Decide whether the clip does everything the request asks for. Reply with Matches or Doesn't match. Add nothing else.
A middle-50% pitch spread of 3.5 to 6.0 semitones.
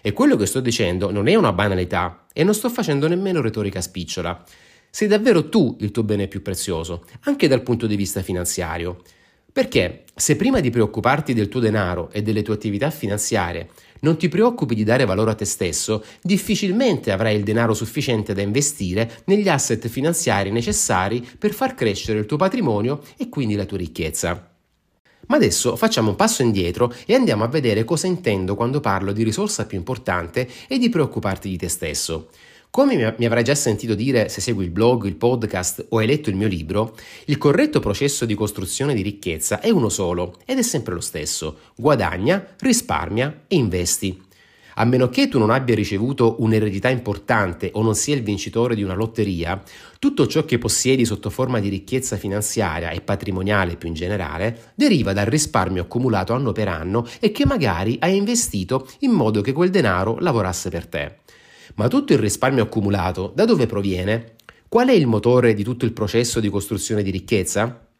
Matches